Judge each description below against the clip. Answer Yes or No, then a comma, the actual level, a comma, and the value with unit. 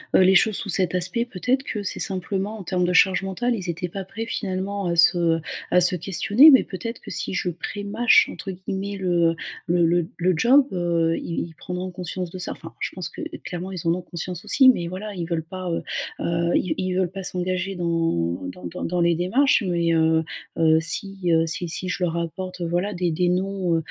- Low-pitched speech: No, medium, 180 Hz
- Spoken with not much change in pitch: Yes, narrow, 2.3 semitones